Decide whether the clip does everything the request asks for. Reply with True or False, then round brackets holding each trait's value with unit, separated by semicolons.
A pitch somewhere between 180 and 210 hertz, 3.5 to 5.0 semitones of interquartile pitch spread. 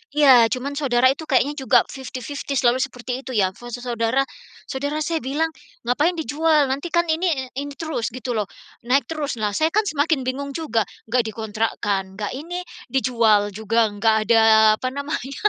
False (260 Hz; 4.1 semitones)